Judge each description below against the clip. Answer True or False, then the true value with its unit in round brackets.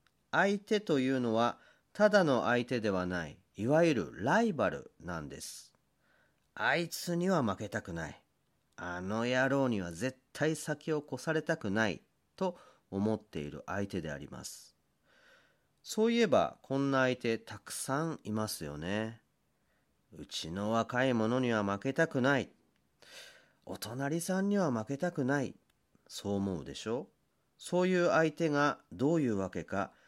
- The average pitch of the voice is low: True (130 Hz)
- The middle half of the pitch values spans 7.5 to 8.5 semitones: True (7.8 semitones)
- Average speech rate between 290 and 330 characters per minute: False (270 characters per minute)